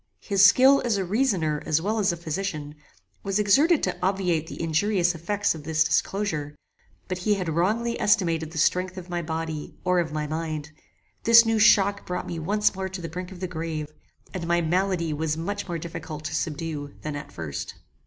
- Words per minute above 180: Yes, average, 195 wpm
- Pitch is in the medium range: Yes, medium, 175 Hz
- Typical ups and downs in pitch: Yes, average, 3.9 semitones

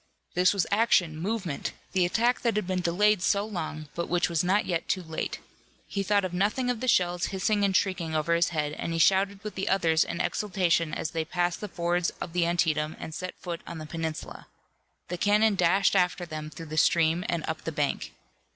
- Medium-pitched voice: Yes, medium, 175 Hz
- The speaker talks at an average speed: No, fast, 210 wpm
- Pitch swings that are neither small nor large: Yes, average, 3.2 semitones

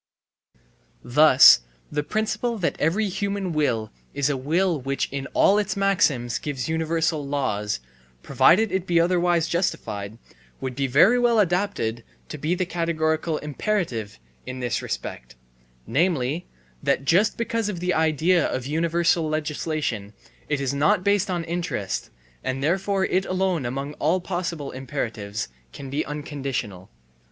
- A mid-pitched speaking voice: Yes, medium, 155 Hz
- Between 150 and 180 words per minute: No, average, 140 wpm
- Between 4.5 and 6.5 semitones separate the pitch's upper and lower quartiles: Yes, wide, 5.4 semitones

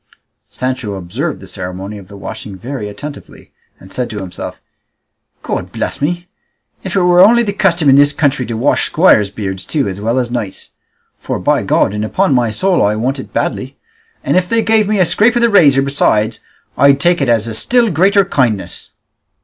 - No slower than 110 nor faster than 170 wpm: No, average, 200 wpm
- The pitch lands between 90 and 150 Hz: Yes, low, 135 Hz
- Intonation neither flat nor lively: No, wide, 8.8 semitones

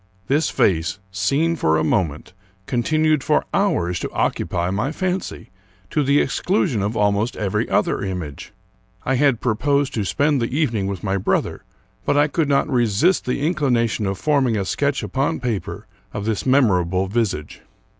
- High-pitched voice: No, low, 120 Hz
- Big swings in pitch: Yes, wide, 6.7 semitones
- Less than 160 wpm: No, average, 165 wpm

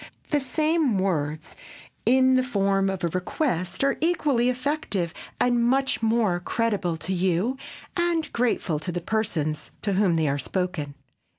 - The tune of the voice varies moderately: No, wide, 6.6 semitones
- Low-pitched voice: No, high, 205 Hz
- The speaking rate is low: No, average, 160 wpm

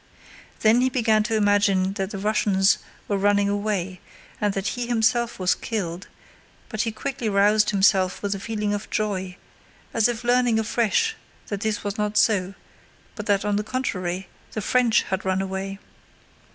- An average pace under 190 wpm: Yes, average, 165 wpm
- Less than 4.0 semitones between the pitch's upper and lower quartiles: Yes, narrow, 2.4 semitones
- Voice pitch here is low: No, high, 205 Hz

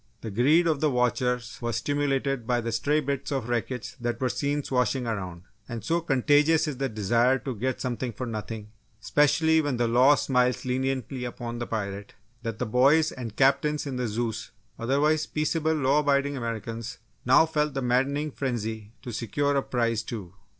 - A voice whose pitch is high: No, low, 125 Hz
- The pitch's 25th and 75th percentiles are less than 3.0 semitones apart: No, average, 3.6 semitones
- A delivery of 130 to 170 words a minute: No, average, 180 wpm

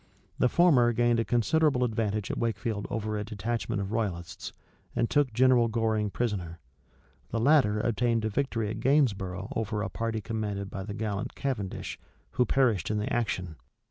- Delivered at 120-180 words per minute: Yes, average, 165 wpm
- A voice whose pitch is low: Yes, low, 110 Hz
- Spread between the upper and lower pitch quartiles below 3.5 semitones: Yes, average, 2.7 semitones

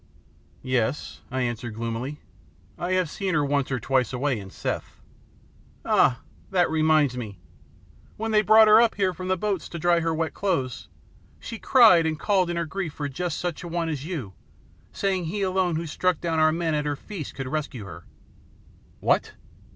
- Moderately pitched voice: Yes, medium, 160 Hz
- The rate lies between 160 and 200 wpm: Yes, average, 190 wpm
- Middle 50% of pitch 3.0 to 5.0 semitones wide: No, wide, 5.5 semitones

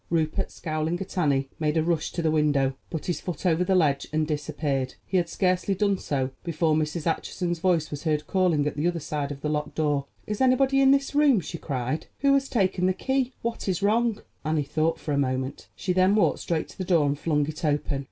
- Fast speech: Yes, fast, 230 wpm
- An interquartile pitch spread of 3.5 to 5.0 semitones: Yes, average, 4.0 semitones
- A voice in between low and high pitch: Yes, medium, 160 Hz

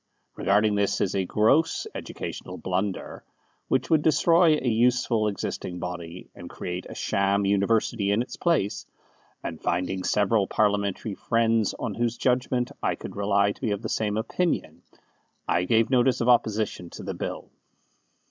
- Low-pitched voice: Yes, low, 105 Hz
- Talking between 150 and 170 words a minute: Yes, average, 155 wpm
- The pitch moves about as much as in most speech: Yes, average, 3.4 semitones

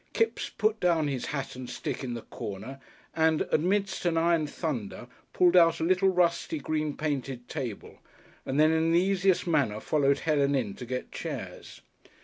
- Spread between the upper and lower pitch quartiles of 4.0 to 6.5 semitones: Yes, average, 4.3 semitones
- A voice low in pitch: No, medium, 155 Hz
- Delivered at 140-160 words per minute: No, average, 170 wpm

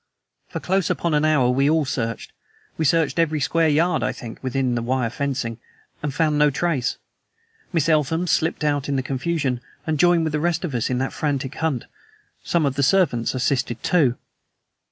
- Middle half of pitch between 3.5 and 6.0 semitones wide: Yes, average, 3.8 semitones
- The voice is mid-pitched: Yes, medium, 145 Hz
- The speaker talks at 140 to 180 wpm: No, average, 190 wpm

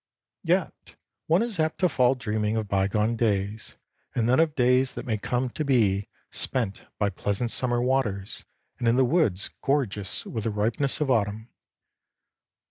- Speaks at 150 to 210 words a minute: Yes, average, 160 wpm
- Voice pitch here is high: No, low, 115 Hz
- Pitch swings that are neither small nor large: Yes, average, 4.1 semitones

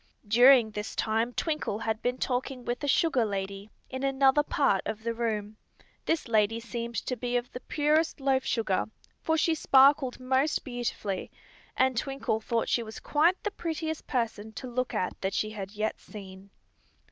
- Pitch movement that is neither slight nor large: Yes, average, 3.8 semitones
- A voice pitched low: No, high, 245 Hz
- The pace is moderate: Yes, average, 170 wpm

